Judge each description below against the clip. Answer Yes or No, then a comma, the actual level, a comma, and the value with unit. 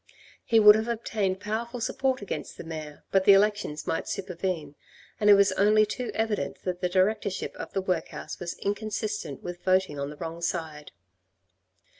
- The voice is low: No, high, 195 Hz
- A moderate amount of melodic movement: Yes, average, 3.8 semitones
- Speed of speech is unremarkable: Yes, average, 170 wpm